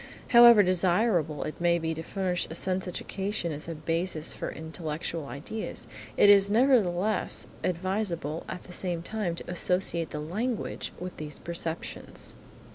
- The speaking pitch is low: No, medium, 175 Hz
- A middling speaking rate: Yes, average, 145 wpm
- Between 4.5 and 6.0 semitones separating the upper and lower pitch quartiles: No, average, 3.3 semitones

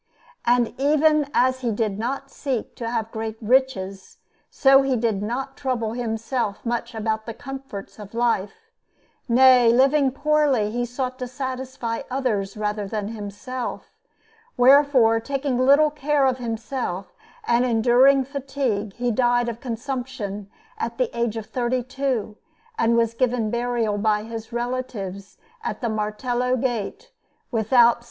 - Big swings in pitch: No, average, 3.0 semitones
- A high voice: Yes, high, 240 Hz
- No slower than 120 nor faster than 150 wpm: Yes, average, 140 wpm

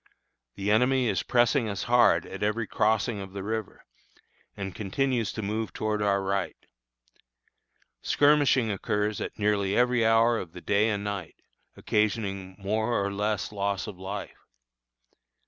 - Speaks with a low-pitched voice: Yes, low, 105 Hz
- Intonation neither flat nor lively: No, narrow, 2.3 semitones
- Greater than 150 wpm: No, average, 145 wpm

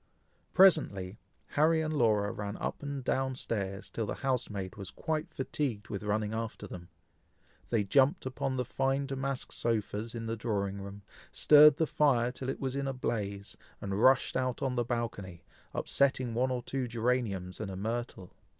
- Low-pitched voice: Yes, low, 120 Hz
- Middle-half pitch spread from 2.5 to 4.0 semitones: No, average, 4.6 semitones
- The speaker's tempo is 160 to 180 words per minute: Yes, average, 170 wpm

